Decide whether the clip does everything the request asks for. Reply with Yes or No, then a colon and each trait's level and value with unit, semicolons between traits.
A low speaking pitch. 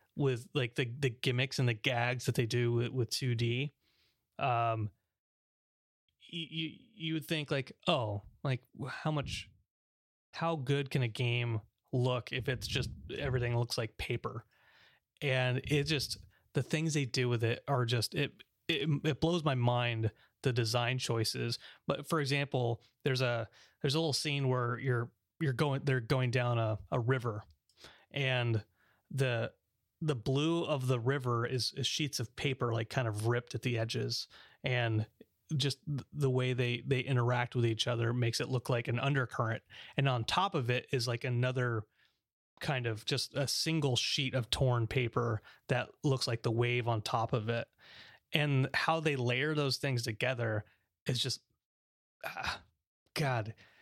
Yes: low, 125 Hz